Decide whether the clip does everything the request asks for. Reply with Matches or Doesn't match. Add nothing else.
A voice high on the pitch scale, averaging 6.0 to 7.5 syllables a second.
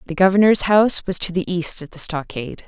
Doesn't match